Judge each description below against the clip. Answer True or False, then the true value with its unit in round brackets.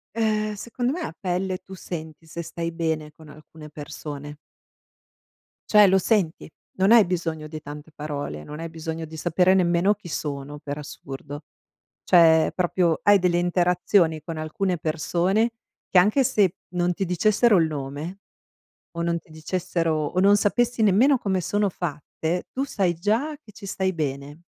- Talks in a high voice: False (175 Hz)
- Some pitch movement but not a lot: True (3.8 semitones)